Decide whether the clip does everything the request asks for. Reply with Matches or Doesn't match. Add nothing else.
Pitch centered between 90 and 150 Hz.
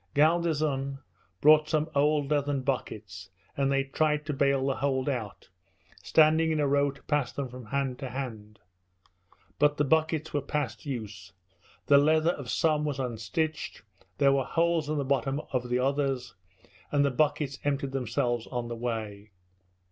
Matches